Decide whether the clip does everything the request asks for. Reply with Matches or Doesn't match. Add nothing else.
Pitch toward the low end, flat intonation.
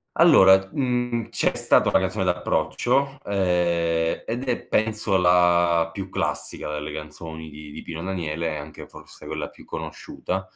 Doesn't match